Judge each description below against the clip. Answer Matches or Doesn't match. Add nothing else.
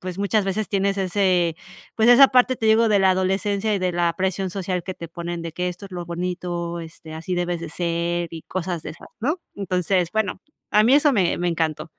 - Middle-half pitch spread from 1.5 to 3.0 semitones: Matches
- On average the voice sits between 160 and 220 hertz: Matches